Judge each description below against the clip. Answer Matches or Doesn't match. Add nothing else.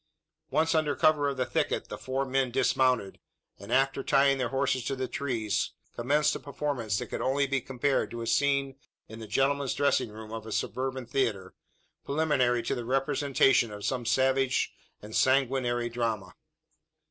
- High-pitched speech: Doesn't match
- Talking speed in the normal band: Matches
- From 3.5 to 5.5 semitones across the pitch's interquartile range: Doesn't match